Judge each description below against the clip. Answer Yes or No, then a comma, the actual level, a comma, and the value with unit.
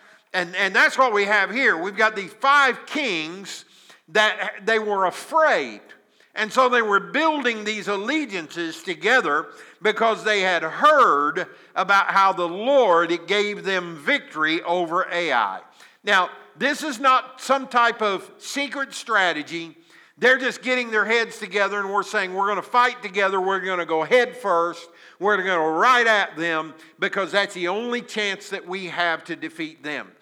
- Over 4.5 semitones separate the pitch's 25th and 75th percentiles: Yes, wide, 5.6 semitones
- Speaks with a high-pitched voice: Yes, high, 205 Hz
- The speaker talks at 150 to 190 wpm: Yes, average, 165 wpm